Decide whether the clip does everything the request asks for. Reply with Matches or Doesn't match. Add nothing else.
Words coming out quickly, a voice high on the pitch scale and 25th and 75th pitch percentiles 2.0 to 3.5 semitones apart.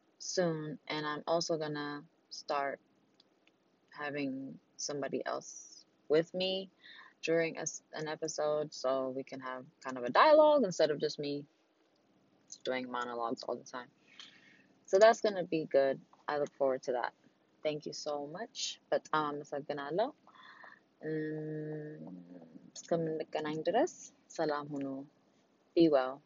Doesn't match